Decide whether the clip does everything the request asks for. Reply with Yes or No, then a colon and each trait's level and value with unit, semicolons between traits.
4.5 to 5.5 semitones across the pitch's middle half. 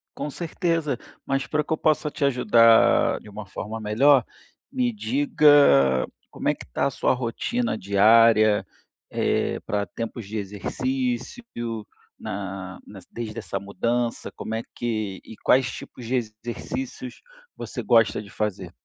Yes: average, 4.9 semitones